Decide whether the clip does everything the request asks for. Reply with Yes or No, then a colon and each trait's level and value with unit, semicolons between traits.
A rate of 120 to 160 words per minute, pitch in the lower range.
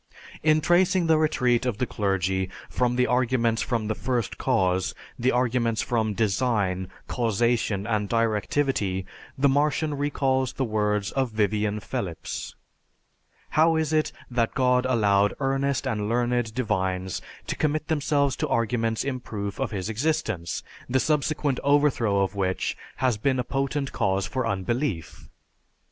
Yes: average, 140 wpm; low, 120 Hz